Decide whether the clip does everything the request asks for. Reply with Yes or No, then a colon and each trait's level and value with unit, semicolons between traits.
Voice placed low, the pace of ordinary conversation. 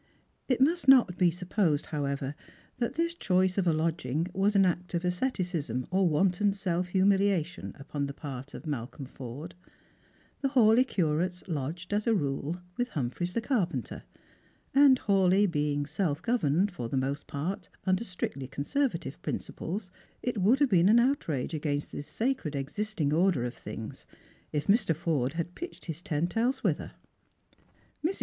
No: medium, 180 Hz; average, 155 wpm